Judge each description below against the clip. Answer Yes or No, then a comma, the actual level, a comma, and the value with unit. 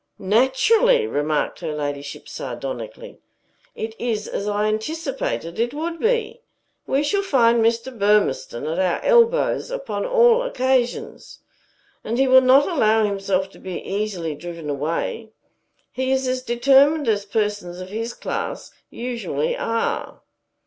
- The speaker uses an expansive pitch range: Yes, wide, 6.7 semitones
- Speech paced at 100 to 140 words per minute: Yes, slow, 135 wpm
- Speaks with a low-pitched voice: No, high, 235 Hz